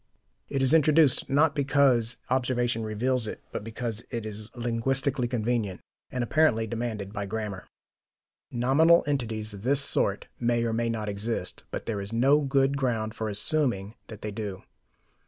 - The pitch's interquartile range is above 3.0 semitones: Yes, average, 3.7 semitones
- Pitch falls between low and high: No, low, 120 Hz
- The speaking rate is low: No, average, 155 wpm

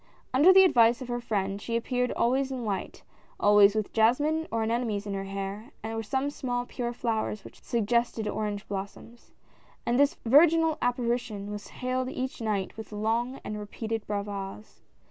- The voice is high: Yes, high, 230 Hz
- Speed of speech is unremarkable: Yes, average, 170 wpm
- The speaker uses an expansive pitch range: No, average, 3.3 semitones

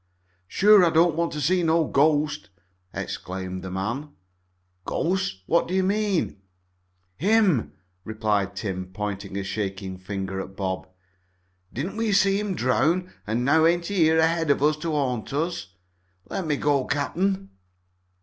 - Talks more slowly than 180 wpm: Yes, average, 150 wpm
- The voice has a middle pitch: Yes, medium, 150 Hz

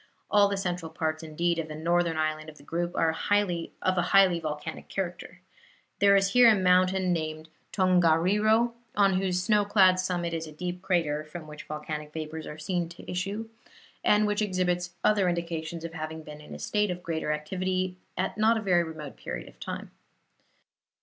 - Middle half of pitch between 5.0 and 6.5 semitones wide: No, average, 3.1 semitones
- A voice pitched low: No, medium, 175 Hz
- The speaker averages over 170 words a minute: Yes, average, 185 wpm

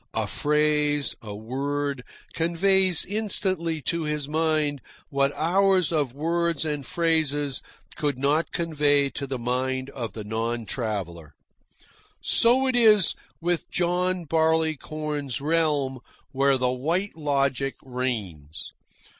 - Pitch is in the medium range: Yes, medium, 145 Hz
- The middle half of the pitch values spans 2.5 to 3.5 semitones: No, average, 4.0 semitones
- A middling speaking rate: No, slow, 115 wpm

